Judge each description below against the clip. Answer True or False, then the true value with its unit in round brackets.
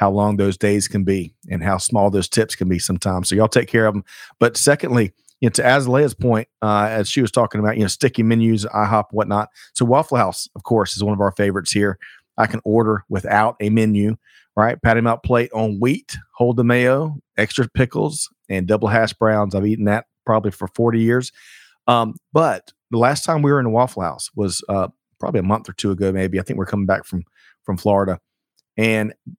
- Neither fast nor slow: False (220 wpm)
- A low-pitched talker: True (110 Hz)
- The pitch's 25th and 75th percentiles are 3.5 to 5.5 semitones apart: False (2.8 semitones)